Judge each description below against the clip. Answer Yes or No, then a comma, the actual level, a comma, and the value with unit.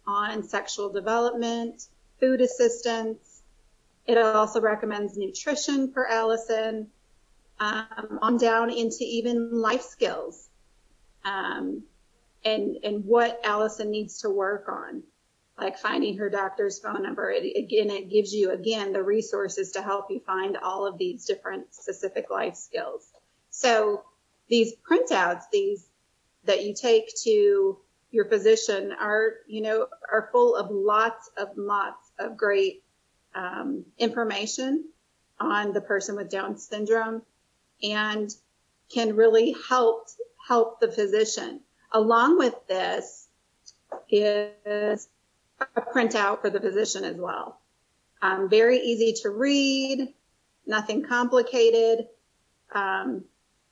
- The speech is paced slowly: Yes, slow, 120 wpm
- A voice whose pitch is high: Yes, high, 225 Hz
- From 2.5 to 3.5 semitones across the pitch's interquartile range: No, average, 4.3 semitones